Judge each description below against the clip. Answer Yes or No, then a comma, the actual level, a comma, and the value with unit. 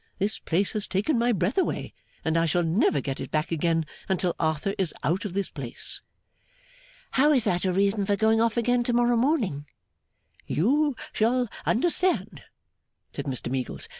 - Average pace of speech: Yes, average, 170 wpm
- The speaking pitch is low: No, high, 200 Hz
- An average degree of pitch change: No, wide, 6.3 semitones